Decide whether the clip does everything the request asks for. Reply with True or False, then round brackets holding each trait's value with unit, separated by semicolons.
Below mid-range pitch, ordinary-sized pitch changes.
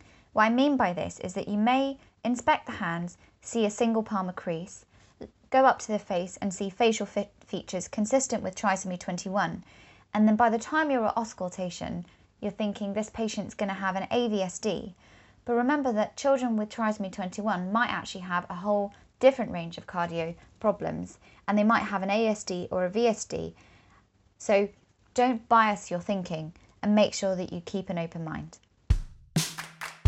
False (205 Hz; 3.7 semitones)